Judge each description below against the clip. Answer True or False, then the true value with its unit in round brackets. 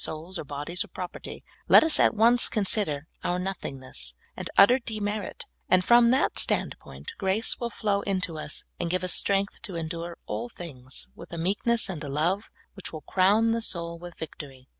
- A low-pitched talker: False (185 Hz)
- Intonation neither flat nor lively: True (4.8 semitones)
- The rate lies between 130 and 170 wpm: False (185 wpm)